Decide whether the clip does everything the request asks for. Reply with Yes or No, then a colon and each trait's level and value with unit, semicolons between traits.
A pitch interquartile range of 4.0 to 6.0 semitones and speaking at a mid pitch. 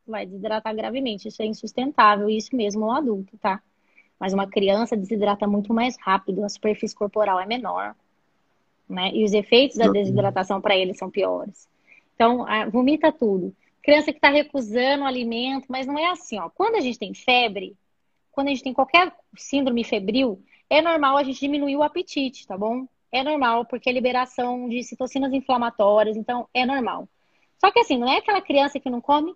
No: average, 4.4 semitones; high, 245 Hz